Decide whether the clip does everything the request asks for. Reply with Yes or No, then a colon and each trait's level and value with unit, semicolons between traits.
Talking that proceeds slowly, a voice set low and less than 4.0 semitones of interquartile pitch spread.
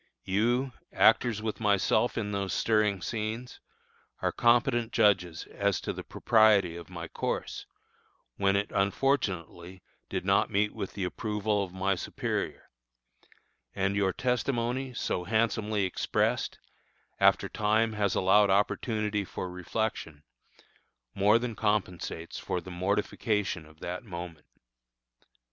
Yes: slow, 120 wpm; low, 105 Hz; average, 3.1 semitones